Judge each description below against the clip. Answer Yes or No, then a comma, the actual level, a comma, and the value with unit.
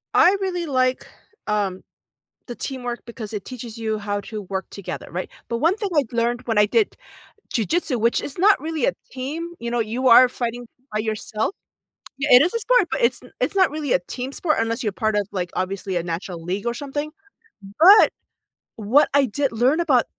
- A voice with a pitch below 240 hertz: No, high, 245 Hz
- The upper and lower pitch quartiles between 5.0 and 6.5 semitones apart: Yes, wide, 5.4 semitones